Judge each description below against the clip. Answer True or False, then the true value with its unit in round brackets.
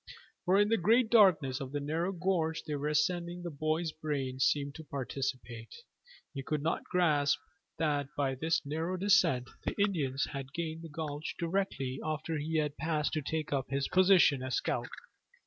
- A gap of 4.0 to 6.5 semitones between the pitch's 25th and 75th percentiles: False (3.5 semitones)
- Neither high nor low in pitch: True (155 Hz)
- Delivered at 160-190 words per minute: True (175 wpm)